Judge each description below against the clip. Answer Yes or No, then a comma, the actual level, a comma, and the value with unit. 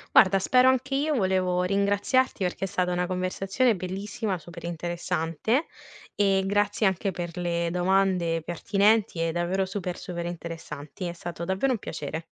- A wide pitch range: No, average, 2.7 semitones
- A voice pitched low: No, medium, 185 Hz